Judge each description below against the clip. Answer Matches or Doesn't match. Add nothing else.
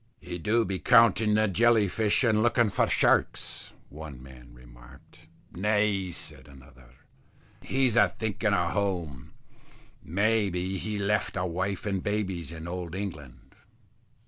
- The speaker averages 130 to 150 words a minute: Matches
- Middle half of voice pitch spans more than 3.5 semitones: Matches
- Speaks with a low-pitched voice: Matches